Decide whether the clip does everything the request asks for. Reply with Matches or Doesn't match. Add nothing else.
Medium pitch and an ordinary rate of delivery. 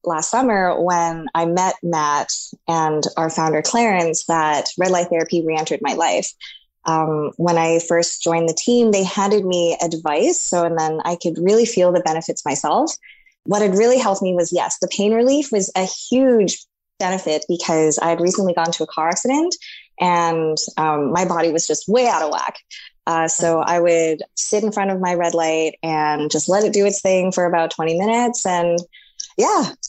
Matches